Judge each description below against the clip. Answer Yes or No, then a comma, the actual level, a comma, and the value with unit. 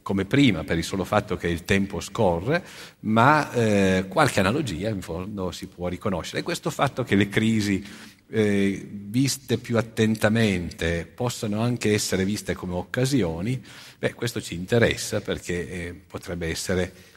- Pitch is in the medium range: No, low, 100 Hz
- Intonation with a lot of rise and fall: No, average, 3.9 semitones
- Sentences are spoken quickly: No, average, 150 wpm